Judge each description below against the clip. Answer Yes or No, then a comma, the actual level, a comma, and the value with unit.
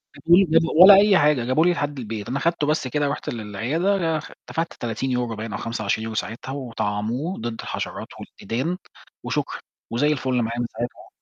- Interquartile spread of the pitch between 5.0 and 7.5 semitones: Yes, wide, 5.6 semitones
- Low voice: Yes, low, 130 Hz